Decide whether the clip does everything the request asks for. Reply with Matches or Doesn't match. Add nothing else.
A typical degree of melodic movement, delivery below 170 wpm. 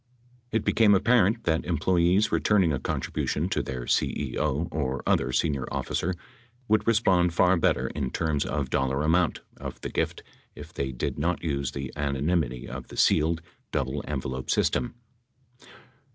Matches